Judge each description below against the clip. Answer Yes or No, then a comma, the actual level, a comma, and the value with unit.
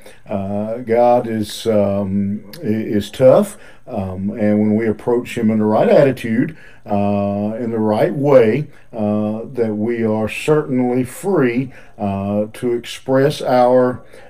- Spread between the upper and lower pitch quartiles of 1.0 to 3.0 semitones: Yes, average, 2.7 semitones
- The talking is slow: Yes, slow, 130 wpm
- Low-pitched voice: Yes, low, 110 Hz